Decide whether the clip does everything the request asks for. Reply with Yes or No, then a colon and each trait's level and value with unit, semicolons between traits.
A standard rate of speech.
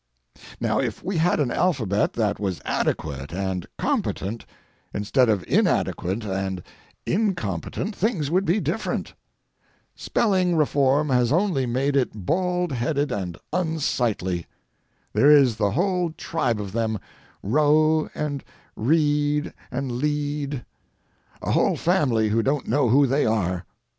No: slow, 125 wpm